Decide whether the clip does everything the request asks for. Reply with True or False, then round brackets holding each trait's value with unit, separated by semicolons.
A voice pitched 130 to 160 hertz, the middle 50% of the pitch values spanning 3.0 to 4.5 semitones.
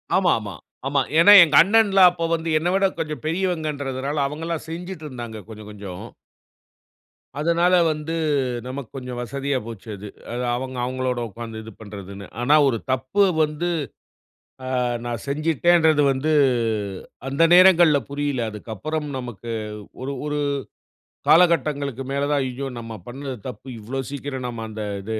False (140 Hz; 4.9 semitones)